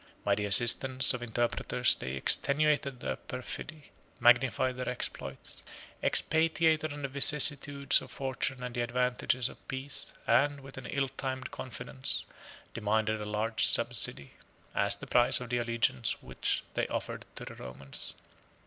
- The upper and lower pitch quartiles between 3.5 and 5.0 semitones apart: No, average, 2.9 semitones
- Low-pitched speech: Yes, low, 125 Hz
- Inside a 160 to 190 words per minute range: No, average, 145 wpm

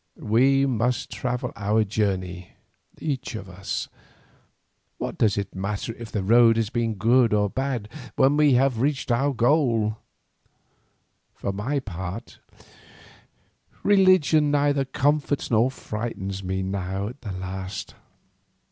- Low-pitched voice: Yes, low, 115 Hz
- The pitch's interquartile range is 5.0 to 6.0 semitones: Yes, average, 5.3 semitones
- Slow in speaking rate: Yes, slow, 125 wpm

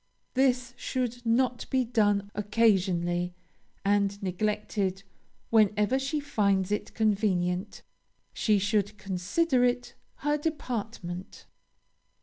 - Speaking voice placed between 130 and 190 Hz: No, high, 210 Hz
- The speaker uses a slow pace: Yes, slow, 95 wpm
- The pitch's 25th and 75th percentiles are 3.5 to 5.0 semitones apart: Yes, average, 4.0 semitones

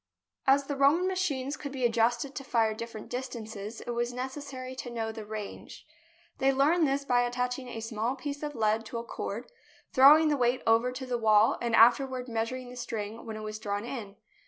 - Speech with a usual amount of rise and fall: Yes, average, 3.1 semitones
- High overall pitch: Yes, high, 245 Hz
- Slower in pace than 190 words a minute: No, average, 200 wpm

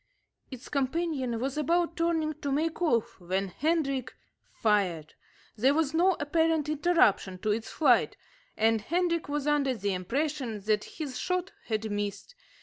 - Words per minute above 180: No, average, 145 wpm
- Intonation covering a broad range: Yes, wide, 6.9 semitones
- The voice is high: Yes, very high, 275 Hz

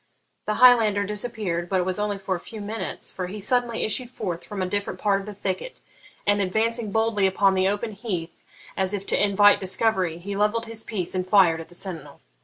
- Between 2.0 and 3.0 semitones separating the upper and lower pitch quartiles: Yes, average, 2.7 semitones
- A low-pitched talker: No, high, 200 Hz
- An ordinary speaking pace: No, fast, 210 wpm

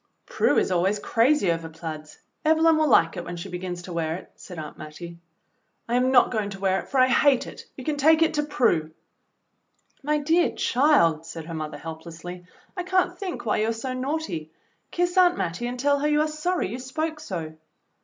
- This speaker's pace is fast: Yes, fast, 210 wpm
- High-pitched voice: Yes, high, 235 Hz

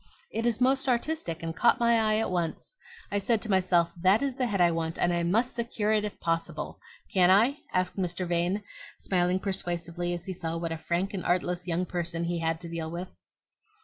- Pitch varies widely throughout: No, average, 4.0 semitones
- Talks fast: Yes, fast, 215 wpm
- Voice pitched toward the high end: No, medium, 180 Hz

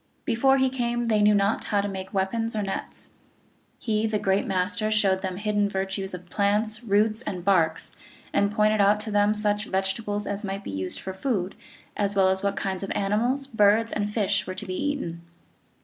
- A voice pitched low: No, high, 205 Hz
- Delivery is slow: No, fast, 205 wpm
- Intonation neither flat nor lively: No, narrow, 2.1 semitones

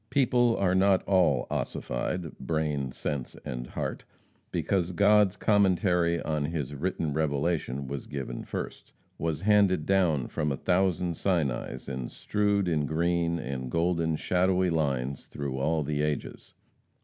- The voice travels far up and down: No, average, 4.5 semitones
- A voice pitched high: No, very low, 80 Hz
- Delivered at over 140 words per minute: No, slow, 135 wpm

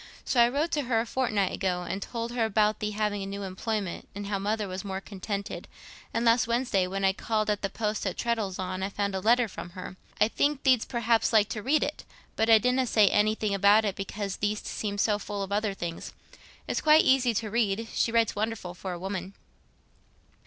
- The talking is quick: Yes, fast, 215 wpm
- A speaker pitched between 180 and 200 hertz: No, high, 210 Hz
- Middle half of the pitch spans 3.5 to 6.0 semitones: No, average, 2.7 semitones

